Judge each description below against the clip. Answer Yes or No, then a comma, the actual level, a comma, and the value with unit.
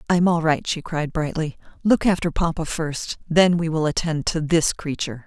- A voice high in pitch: No, medium, 160 Hz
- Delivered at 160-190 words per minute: No, fast, 205 wpm